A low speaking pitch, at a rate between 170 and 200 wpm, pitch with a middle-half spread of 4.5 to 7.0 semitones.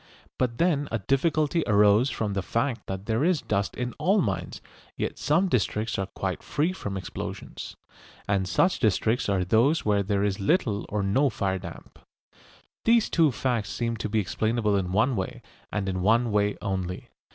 Yes: low, 110 Hz; average, 175 wpm; average, 5.1 semitones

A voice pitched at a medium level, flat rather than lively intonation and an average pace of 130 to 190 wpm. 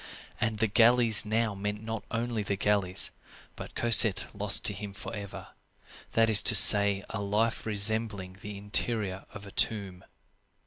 No: low, 105 Hz; narrow, 2.0 semitones; average, 150 wpm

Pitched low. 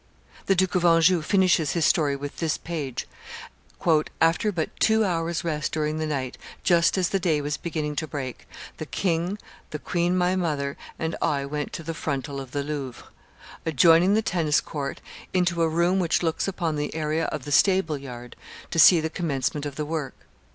No: medium, 160 Hz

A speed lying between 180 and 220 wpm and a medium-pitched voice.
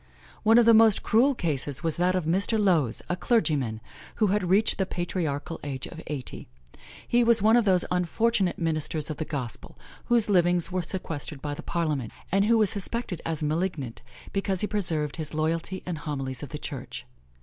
Yes: average, 190 wpm; medium, 175 Hz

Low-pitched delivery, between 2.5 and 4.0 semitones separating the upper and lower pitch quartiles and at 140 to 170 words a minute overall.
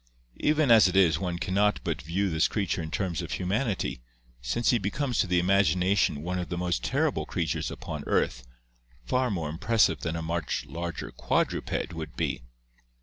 No: very low, 90 Hz; average, 3.4 semitones; average, 190 wpm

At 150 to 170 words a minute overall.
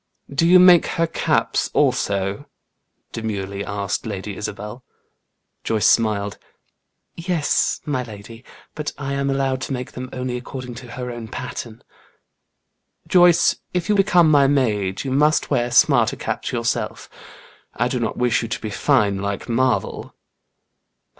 No: average, 140 wpm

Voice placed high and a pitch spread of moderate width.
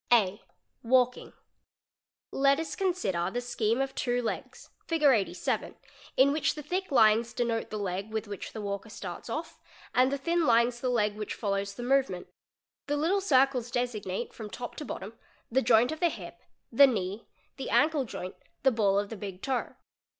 Yes: high, 240 Hz; average, 4.5 semitones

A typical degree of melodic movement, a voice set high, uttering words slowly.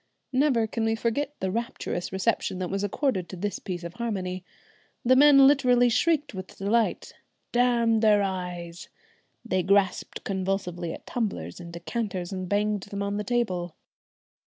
No: average, 4.3 semitones; high, 205 Hz; average, 155 wpm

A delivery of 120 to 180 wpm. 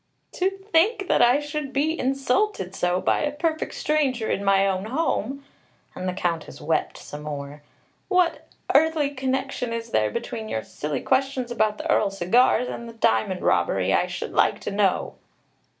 Yes: average, 165 wpm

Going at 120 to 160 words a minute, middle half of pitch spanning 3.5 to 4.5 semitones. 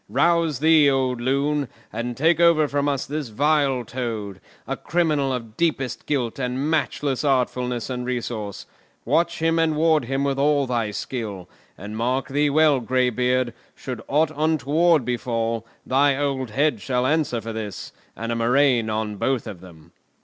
Yes: average, 155 wpm; average, 4.0 semitones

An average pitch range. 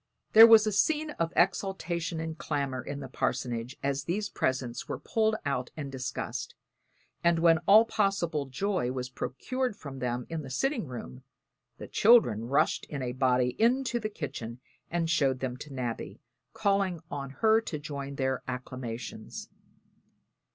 No: wide, 7.5 semitones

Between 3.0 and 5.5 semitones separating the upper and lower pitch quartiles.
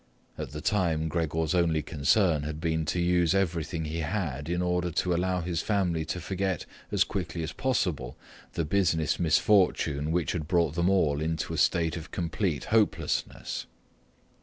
No: narrow, 2.5 semitones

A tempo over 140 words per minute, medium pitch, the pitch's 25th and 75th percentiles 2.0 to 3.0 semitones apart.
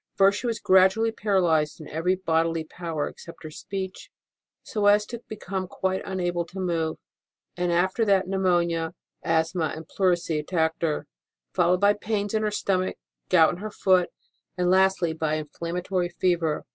Yes: average, 160 wpm; medium, 180 Hz; average, 2.7 semitones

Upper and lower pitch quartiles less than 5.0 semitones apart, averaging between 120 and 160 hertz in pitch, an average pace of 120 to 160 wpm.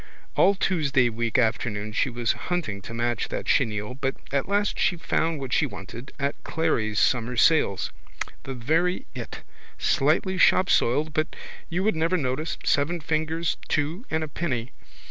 No: wide, 5.5 semitones; medium, 140 Hz; average, 155 wpm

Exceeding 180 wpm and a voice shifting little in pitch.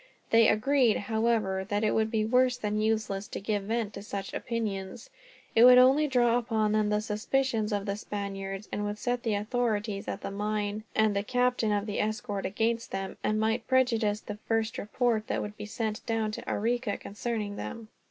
Yes: average, 190 wpm; narrow, 2.1 semitones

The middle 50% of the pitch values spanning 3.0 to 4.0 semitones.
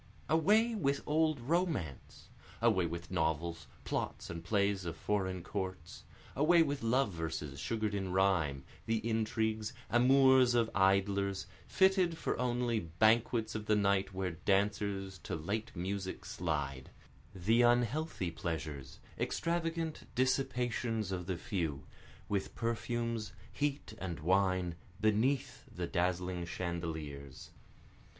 No: wide, 5.5 semitones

